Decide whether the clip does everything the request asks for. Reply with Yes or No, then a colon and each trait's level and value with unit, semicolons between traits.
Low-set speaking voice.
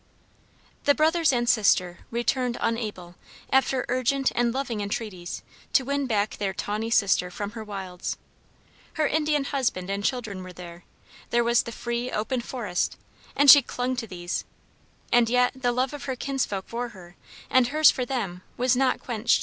No: high, 240 Hz